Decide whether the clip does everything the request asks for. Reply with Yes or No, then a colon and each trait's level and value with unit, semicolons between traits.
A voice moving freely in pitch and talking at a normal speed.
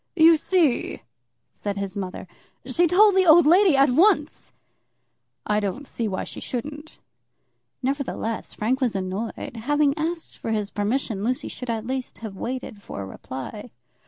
Yes: wide, 6.4 semitones; average, 150 wpm